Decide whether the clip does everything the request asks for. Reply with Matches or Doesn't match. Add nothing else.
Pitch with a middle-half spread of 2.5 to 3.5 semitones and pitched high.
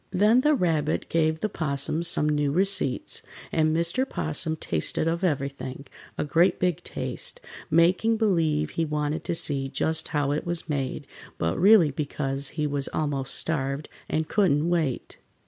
Doesn't match